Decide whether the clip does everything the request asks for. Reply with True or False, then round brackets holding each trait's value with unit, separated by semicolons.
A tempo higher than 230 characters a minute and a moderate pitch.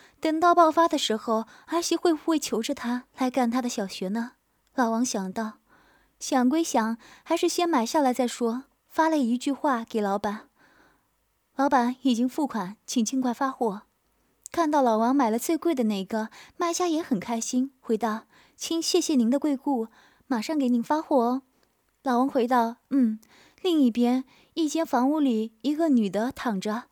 False (240 characters per minute; 255 Hz)